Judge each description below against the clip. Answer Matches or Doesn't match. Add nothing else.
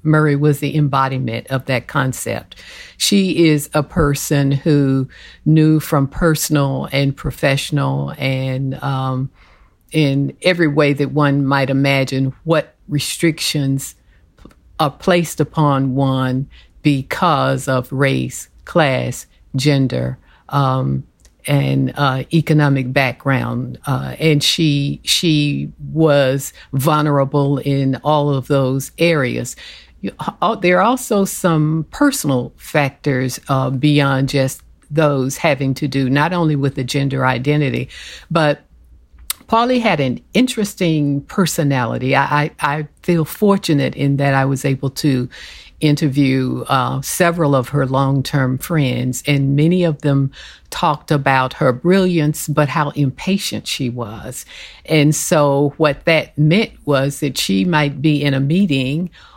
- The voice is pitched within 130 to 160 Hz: Matches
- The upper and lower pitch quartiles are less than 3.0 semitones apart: Matches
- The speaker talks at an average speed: Doesn't match